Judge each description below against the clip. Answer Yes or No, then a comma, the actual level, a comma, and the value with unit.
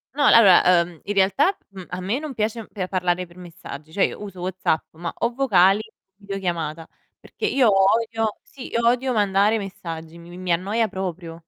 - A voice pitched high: Yes, high, 195 Hz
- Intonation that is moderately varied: Yes, average, 4.2 semitones